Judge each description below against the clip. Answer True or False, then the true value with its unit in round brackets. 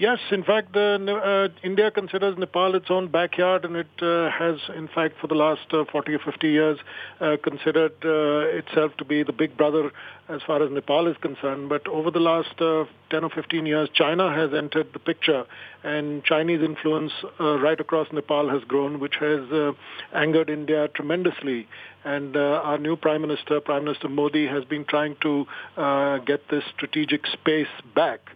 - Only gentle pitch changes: True (1.9 semitones)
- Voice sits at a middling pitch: True (155 Hz)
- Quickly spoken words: False (185 wpm)